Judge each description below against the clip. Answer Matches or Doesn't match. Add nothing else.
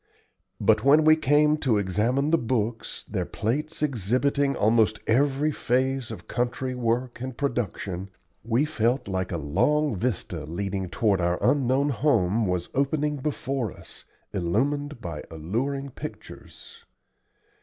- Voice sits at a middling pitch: Doesn't match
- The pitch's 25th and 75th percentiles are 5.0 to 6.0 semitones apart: Matches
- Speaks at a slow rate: Matches